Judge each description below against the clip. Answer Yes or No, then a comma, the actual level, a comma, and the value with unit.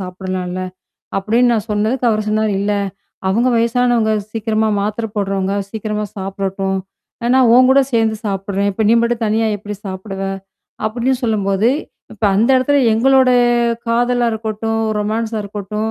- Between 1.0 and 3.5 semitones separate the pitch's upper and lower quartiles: Yes, average, 2.7 semitones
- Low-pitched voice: No, high, 220 Hz